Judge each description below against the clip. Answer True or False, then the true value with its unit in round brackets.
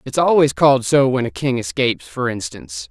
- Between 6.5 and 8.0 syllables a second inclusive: False (5.4 syllables/s)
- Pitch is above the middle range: False (135 Hz)